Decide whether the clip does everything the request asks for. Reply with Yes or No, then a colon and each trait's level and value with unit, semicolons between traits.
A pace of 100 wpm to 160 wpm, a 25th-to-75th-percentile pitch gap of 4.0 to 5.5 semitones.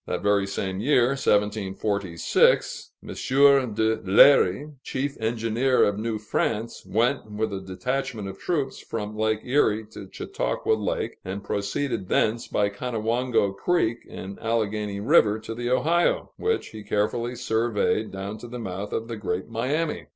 No: average, 145 wpm; average, 3.2 semitones